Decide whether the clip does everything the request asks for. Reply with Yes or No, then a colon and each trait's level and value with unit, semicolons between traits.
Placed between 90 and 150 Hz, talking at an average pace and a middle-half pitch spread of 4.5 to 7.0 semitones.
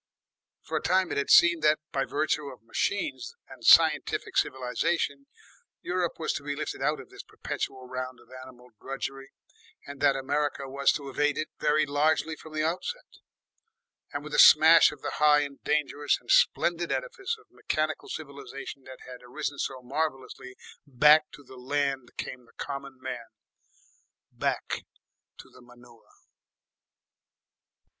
No: medium, 140 Hz; average, 150 wpm; average, 2.8 semitones